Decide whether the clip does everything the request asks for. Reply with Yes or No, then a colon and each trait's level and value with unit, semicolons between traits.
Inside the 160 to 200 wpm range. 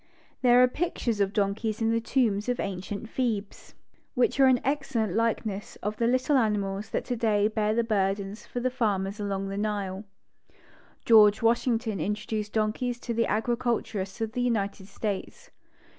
Yes: average, 170 wpm